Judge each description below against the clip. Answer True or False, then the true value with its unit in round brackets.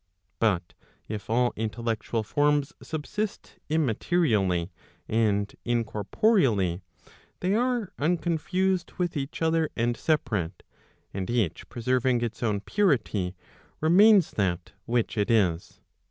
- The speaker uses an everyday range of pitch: False (7.6 semitones)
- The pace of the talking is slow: True (105 wpm)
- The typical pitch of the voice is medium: False (120 Hz)